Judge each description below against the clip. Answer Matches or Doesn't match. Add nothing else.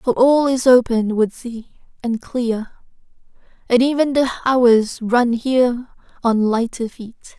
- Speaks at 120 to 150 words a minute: Matches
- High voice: Matches